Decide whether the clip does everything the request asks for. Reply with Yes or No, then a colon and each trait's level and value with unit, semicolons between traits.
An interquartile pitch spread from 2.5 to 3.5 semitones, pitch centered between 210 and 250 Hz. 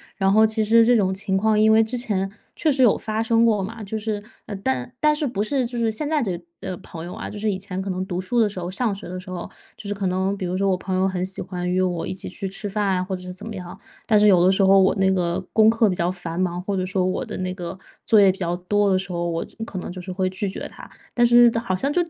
No: average, 3.0 semitones; high, 195 Hz